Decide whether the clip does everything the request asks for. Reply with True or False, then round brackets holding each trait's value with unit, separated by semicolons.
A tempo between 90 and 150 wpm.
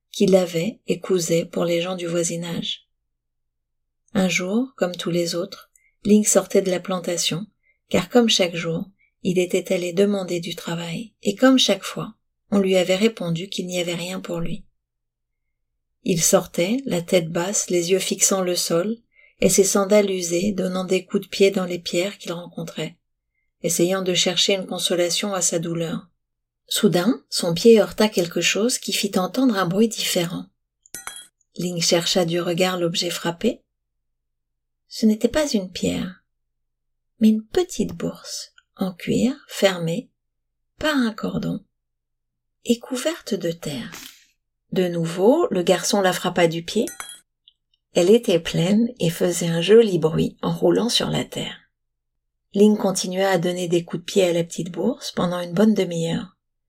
False (160 wpm)